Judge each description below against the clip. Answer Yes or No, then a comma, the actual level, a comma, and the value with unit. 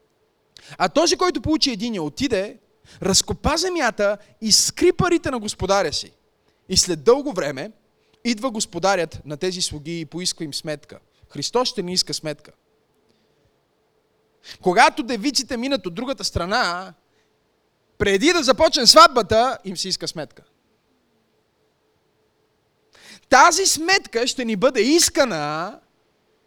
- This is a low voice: No, high, 230 Hz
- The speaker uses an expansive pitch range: Yes, wide, 8.0 semitones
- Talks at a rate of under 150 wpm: Yes, average, 120 wpm